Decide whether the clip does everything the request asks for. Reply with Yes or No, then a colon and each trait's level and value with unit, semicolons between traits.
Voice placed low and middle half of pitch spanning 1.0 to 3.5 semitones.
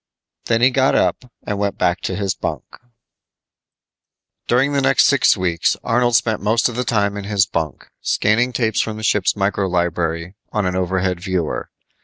No: low, 100 Hz; average, 4.2 semitones